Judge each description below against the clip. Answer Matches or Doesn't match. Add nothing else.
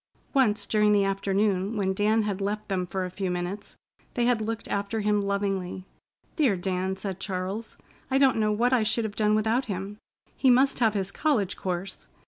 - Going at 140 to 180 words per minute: Doesn't match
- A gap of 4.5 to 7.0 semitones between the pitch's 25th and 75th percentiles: Doesn't match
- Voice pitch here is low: Doesn't match